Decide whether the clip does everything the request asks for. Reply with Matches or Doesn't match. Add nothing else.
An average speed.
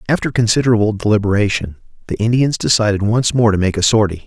Matches